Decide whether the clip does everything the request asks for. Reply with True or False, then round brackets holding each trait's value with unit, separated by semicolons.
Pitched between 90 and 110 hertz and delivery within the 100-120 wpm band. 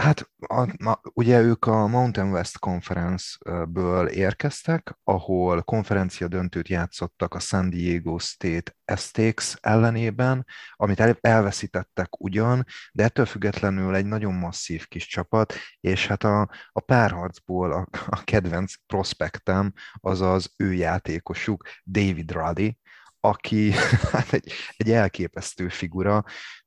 True (95 Hz; 115 wpm)